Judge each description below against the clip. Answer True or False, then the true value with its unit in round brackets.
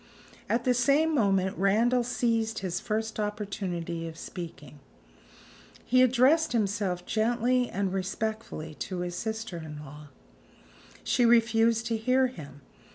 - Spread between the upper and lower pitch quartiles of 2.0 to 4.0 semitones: False (5.0 semitones)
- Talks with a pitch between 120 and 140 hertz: False (220 Hz)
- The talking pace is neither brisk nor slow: False (125 wpm)